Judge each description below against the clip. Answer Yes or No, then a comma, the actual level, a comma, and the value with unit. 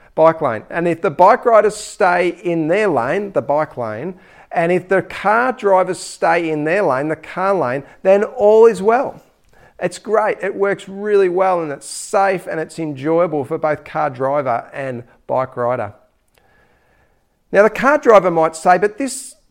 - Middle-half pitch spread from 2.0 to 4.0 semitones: No, average, 4.4 semitones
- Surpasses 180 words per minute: No, average, 175 wpm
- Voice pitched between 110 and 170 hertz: No, medium, 180 Hz